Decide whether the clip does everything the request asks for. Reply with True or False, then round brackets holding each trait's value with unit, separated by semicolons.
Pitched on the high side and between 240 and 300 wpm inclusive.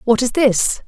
False (240 Hz; 205 wpm)